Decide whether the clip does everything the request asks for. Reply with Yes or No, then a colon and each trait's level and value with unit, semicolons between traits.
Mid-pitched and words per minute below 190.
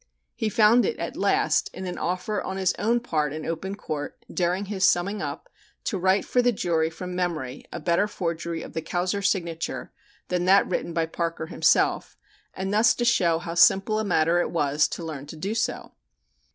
No: medium, 180 Hz; average, 195 wpm